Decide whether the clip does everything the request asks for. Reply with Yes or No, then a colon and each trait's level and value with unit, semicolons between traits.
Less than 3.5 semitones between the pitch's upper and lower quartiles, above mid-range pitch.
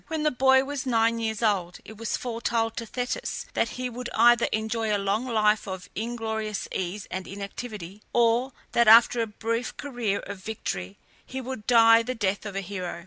Yes: average, 2.8 semitones; high, 225 Hz